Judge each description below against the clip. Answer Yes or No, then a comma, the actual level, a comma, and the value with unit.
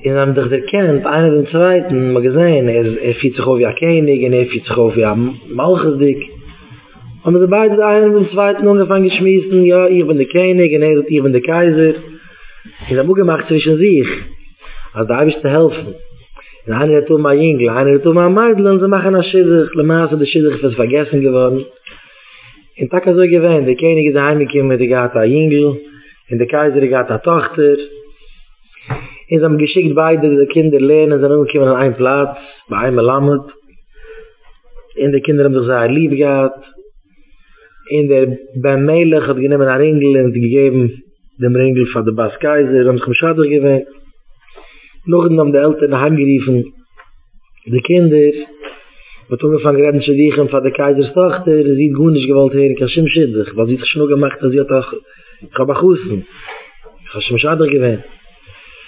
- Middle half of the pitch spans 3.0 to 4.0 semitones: Yes, average, 3.5 semitones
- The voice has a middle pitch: Yes, medium, 145 Hz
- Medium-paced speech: Yes, average, 165 wpm